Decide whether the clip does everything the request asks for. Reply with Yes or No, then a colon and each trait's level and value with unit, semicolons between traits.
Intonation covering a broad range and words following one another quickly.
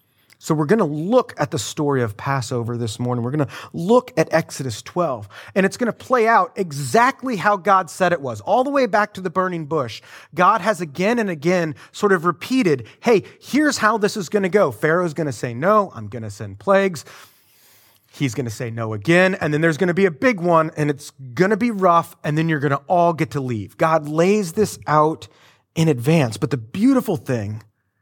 Yes: wide, 7.1 semitones; fast, 225 wpm